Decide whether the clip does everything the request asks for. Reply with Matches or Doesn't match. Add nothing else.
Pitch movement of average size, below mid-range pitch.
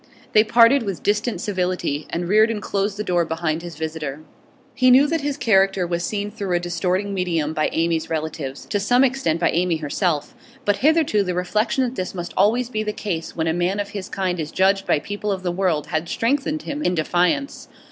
Doesn't match